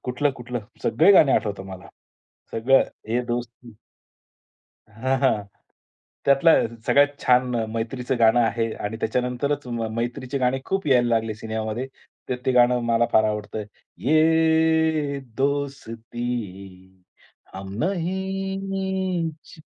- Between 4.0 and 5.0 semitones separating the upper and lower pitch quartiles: Yes, average, 4.3 semitones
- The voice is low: Yes, low, 125 Hz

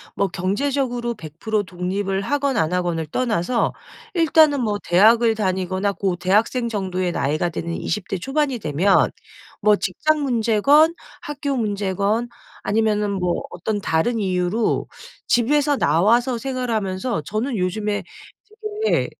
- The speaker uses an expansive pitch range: No, average, 4.9 semitones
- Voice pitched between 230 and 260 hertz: No, high, 210 Hz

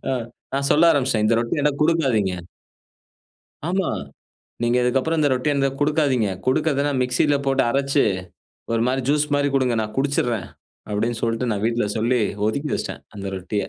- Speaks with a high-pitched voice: No, low, 130 Hz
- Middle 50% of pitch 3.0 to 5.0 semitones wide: Yes, average, 3.8 semitones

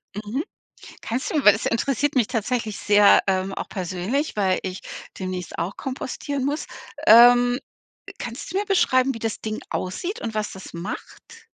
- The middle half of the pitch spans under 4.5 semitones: No, wide, 5.4 semitones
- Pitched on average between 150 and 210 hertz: No, high, 230 Hz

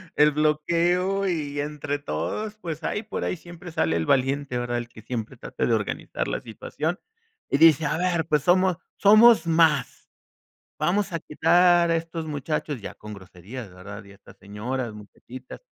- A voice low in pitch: No, medium, 150 Hz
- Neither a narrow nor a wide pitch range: No, wide, 6.2 semitones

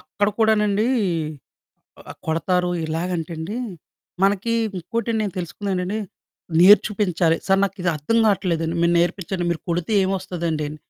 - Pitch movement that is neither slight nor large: Yes, average, 3.2 semitones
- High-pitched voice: No, medium, 180 Hz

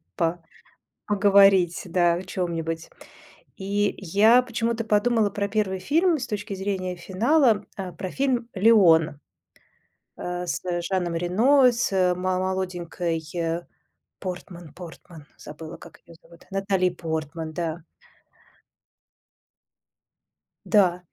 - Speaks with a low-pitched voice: No, medium, 185 Hz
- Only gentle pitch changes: No, average, 3.3 semitones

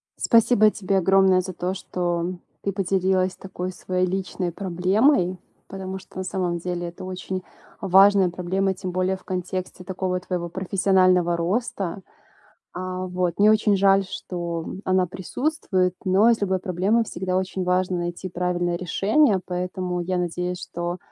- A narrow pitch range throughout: Yes, narrow, 1.3 semitones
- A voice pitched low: No, medium, 185 Hz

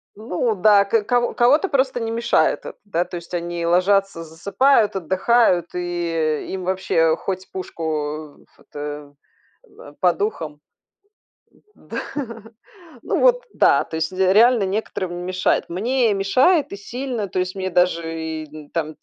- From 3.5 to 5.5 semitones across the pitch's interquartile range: Yes, average, 4.8 semitones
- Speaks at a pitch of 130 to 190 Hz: Yes, medium, 185 Hz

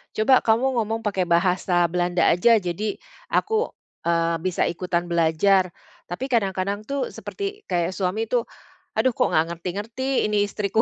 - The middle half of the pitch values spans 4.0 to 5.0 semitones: Yes, average, 4.5 semitones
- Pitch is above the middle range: Yes, high, 200 Hz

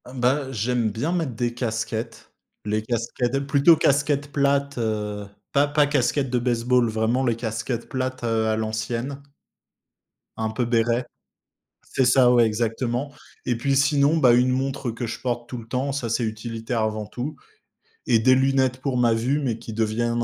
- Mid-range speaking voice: No, low, 120 Hz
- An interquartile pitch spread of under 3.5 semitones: Yes, average, 3.0 semitones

